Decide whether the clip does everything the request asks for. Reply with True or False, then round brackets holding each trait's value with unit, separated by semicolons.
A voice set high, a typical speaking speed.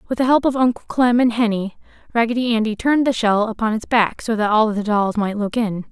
False (225 Hz; 245 wpm)